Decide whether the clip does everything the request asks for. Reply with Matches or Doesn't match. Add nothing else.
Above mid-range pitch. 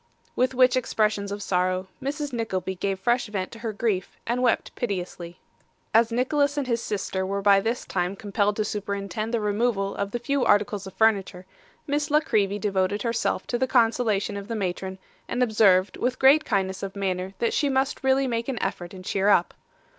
Matches